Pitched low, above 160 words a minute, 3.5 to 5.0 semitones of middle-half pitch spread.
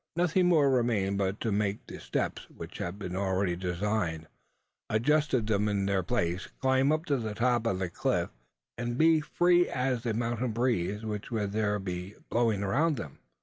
Yes: low, 110 Hz; average, 180 wpm; average, 4.6 semitones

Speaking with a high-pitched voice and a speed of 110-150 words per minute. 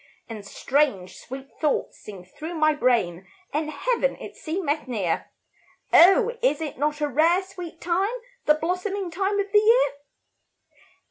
Yes: very high, 310 Hz; average, 145 wpm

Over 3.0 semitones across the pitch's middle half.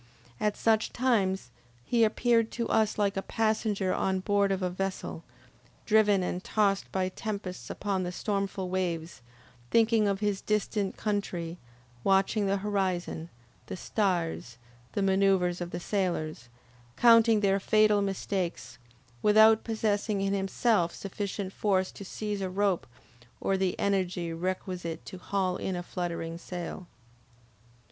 No: narrow, 2.4 semitones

